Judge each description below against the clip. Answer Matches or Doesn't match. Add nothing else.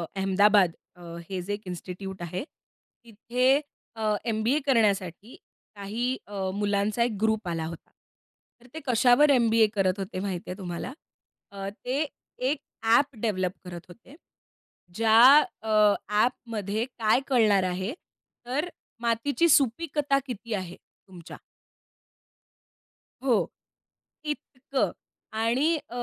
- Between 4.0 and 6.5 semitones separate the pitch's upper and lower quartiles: Matches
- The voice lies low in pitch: Doesn't match